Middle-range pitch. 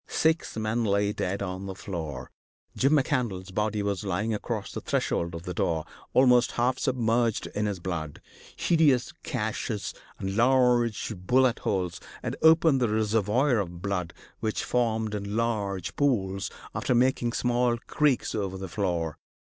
No: low, 110 Hz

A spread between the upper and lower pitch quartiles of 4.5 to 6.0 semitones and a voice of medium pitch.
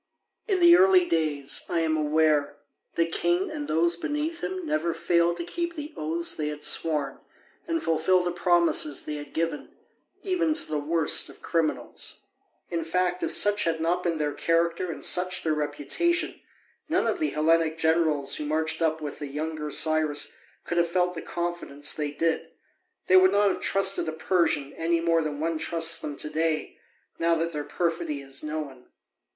No: average, 2.7 semitones; medium, 165 Hz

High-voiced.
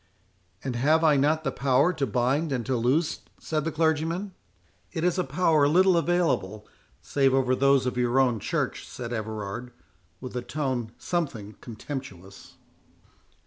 No: low, 135 Hz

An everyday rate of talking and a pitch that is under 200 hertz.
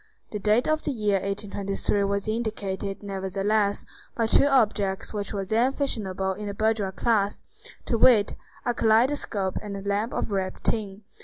No: average, 160 wpm; high, 205 Hz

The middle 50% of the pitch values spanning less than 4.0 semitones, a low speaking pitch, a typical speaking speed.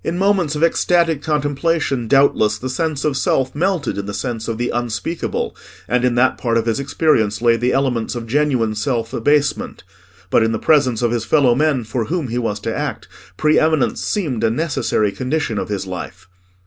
No: average, 4.9 semitones; low, 125 Hz; average, 195 wpm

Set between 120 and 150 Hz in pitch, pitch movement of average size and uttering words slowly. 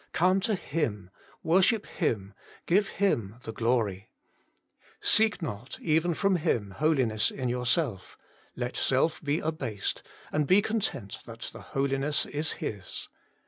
No: medium, 140 Hz; wide, 7.4 semitones; slow, 130 wpm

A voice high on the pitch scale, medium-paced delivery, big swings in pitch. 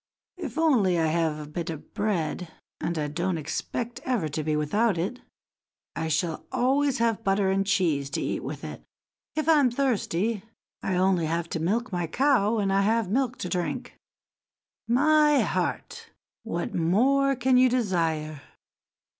Yes: high, 195 Hz; average, 165 wpm; wide, 7.0 semitones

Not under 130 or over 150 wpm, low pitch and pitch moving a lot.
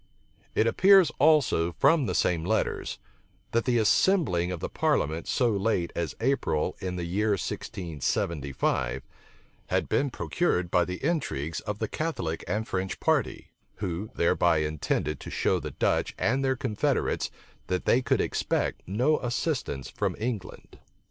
Yes: average, 145 wpm; low, 100 Hz; wide, 7.0 semitones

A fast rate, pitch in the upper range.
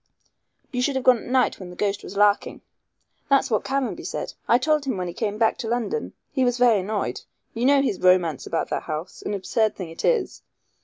Yes: fast, 220 wpm; high, 225 Hz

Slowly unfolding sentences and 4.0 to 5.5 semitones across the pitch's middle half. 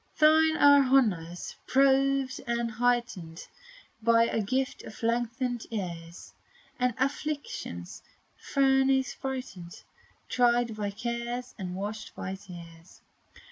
Yes: slow, 100 wpm; average, 5.2 semitones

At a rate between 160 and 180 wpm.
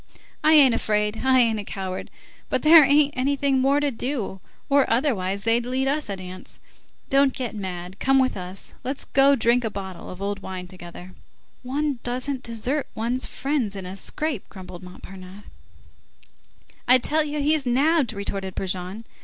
Yes: average, 165 wpm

